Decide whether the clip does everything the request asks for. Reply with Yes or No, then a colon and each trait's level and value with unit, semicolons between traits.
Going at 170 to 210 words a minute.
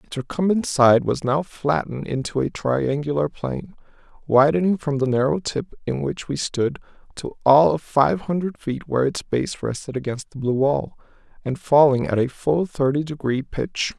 Yes: average, 175 wpm